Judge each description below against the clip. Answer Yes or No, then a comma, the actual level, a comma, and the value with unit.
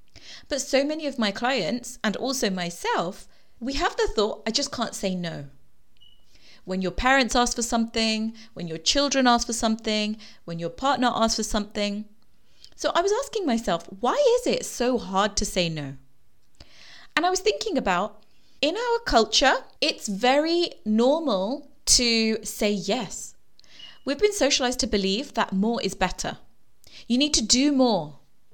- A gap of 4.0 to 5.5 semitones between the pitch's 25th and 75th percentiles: Yes, average, 5.0 semitones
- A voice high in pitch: Yes, high, 230 Hz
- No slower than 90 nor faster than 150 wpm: No, average, 160 wpm